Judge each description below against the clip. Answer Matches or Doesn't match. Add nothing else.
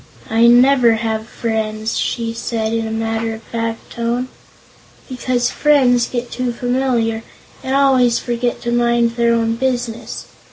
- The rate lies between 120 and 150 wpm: Matches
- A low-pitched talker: Doesn't match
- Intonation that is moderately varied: Doesn't match